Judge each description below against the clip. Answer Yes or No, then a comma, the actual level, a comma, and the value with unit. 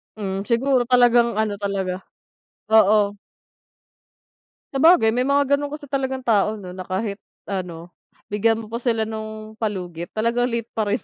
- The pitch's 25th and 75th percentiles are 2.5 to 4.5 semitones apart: Yes, average, 3.3 semitones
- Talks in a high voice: Yes, high, 220 Hz